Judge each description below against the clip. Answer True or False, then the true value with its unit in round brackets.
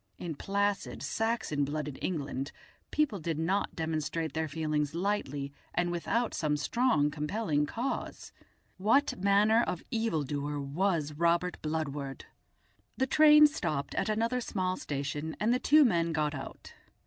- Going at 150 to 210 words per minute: False (135 wpm)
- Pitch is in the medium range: True (165 Hz)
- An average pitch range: False (6.4 semitones)